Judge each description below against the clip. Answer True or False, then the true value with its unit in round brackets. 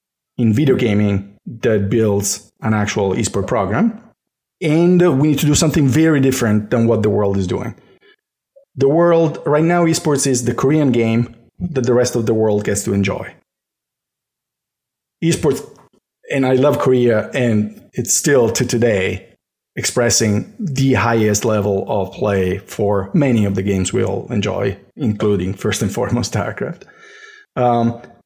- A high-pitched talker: False (120 Hz)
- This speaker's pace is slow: False (150 wpm)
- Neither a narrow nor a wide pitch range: False (6.1 semitones)